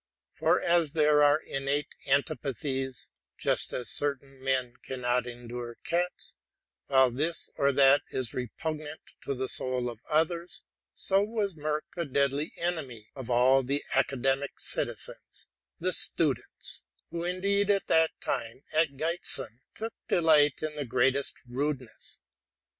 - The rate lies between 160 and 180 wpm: No, slow, 135 wpm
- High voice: No, medium, 140 Hz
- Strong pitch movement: No, average, 3.6 semitones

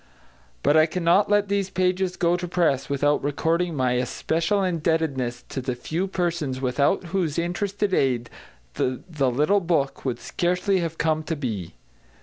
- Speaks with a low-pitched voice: No, medium, 165 Hz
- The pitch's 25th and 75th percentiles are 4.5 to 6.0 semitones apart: Yes, average, 4.9 semitones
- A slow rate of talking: No, average, 150 wpm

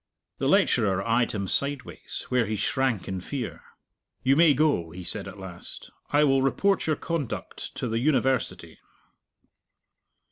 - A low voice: Yes, low, 125 Hz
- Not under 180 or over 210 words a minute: No, average, 145 wpm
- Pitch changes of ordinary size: No, wide, 6.3 semitones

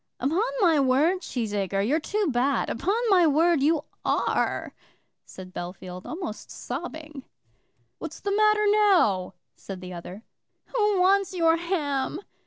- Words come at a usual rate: No, slow, 130 wpm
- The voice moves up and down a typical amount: No, wide, 8.7 semitones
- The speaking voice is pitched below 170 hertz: No, very high, 310 Hz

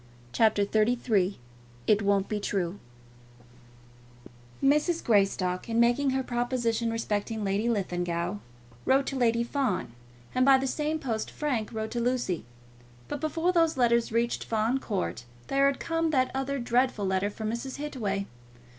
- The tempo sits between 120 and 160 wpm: Yes, average, 145 wpm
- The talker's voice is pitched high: Yes, high, 235 Hz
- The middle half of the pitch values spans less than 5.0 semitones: Yes, average, 4.6 semitones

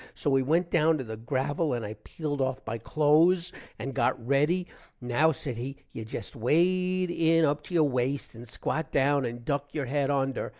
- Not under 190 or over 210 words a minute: Yes, average, 200 wpm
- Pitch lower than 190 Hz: Yes, medium, 140 Hz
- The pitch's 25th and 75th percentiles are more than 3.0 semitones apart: Yes, average, 4.0 semitones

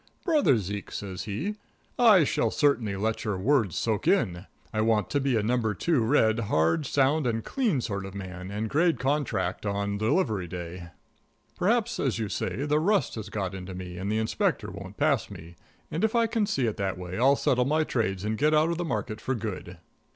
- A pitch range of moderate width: No, wide, 7.1 semitones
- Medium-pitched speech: No, low, 110 Hz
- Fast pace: Yes, fast, 210 wpm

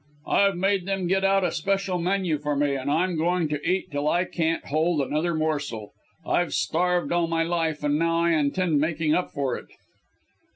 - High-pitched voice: No, medium, 165 Hz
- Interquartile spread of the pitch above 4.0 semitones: No, average, 3.1 semitones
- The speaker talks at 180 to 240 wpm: Yes, average, 195 wpm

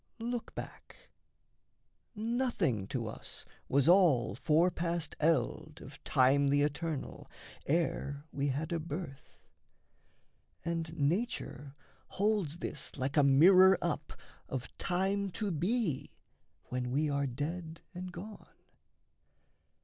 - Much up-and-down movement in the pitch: No, average, 4.5 semitones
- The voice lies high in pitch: No, medium, 155 Hz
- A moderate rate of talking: No, slow, 110 wpm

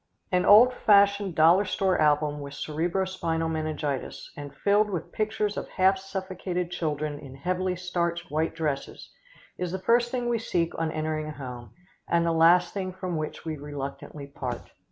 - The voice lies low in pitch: No, medium, 170 Hz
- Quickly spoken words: No, average, 170 wpm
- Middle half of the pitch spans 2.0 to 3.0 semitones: No, average, 3.7 semitones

